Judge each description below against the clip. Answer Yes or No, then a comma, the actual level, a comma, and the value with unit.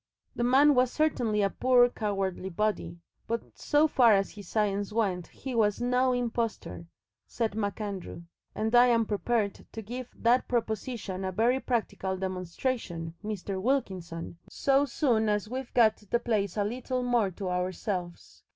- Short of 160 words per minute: Yes, average, 150 wpm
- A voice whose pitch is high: Yes, high, 220 Hz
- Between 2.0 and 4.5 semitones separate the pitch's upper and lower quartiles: Yes, average, 4.1 semitones